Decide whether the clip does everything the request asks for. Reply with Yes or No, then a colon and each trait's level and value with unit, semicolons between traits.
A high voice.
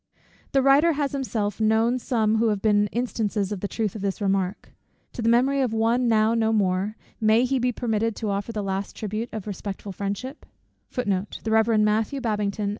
Yes: high, 220 Hz